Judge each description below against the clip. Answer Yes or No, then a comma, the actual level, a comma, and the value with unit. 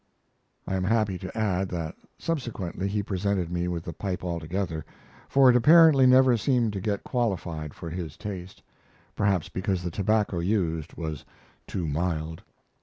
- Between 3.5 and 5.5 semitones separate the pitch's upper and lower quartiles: Yes, average, 4.2 semitones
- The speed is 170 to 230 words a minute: No, average, 155 wpm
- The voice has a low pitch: Yes, very low, 95 Hz